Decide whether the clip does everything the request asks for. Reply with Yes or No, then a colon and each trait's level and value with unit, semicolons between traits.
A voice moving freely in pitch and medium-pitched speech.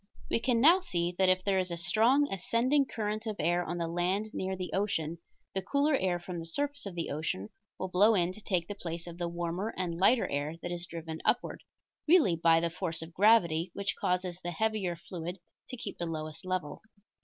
No: average, 3.9 semitones; medium, 180 Hz